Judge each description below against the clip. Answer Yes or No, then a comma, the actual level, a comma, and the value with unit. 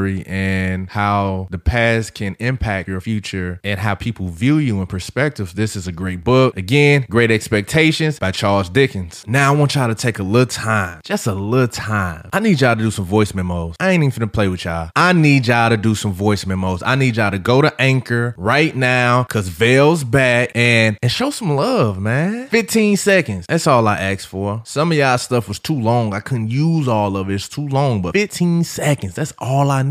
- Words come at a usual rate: No, fast, 225 wpm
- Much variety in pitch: Yes, wide, 5.8 semitones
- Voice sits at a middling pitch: No, low, 115 Hz